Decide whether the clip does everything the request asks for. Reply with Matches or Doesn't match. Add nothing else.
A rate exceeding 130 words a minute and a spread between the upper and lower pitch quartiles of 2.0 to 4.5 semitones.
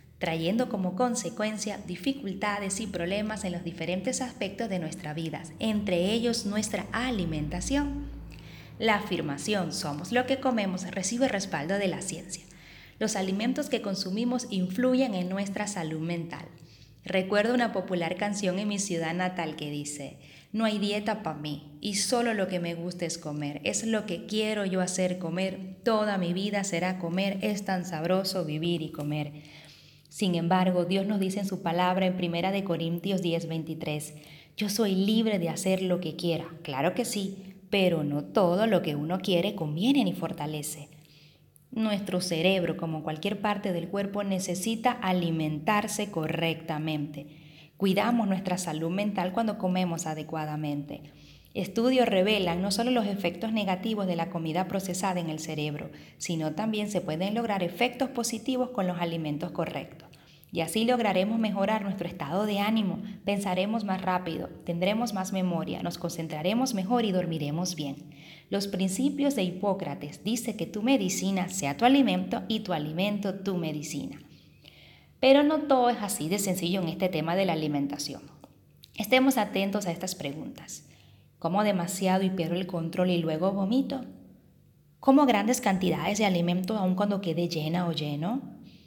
Matches